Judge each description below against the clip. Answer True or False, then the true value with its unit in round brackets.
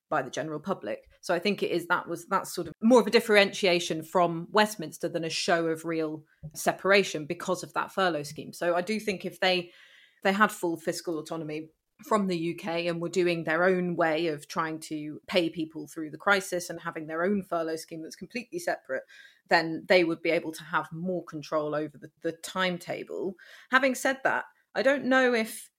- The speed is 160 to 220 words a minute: True (205 wpm)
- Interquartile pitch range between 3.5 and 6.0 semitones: False (2.9 semitones)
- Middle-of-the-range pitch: True (175 Hz)